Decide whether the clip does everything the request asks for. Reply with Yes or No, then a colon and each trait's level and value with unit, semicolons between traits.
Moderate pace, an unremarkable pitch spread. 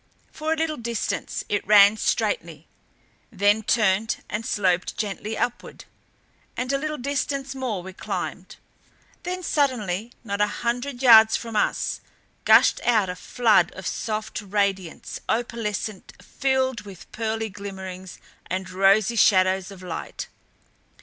No: slow, 130 wpm; average, 4.0 semitones